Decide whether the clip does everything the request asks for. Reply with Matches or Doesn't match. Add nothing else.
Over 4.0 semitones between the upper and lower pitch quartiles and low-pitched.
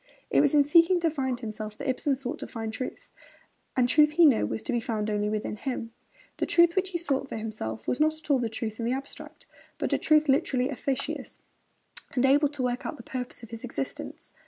Doesn't match